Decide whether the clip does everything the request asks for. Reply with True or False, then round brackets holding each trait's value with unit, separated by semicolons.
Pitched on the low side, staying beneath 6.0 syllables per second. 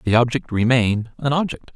True (125 Hz; 5.5 syllables/s)